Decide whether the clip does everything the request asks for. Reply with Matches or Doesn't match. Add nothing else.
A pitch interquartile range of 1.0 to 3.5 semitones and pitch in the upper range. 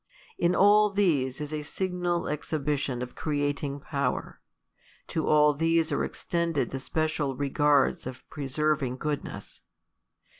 Doesn't match